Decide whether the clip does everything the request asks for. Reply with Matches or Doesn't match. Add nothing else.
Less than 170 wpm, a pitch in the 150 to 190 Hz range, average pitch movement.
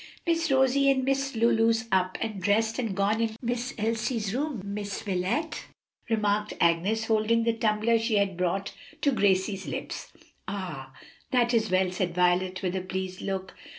Doesn't match